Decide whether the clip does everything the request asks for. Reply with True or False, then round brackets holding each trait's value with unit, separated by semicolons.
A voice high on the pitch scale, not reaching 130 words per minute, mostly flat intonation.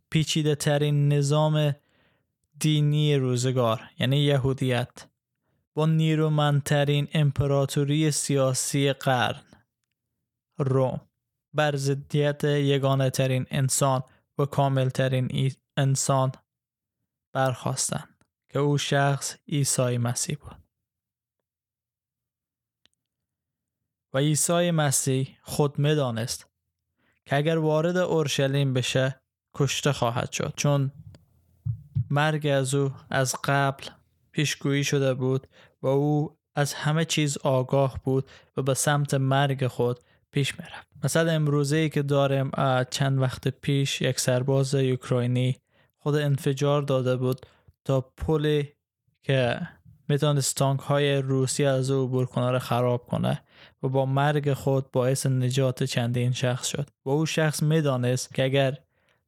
False (135 Hz; 110 wpm; 2.2 semitones)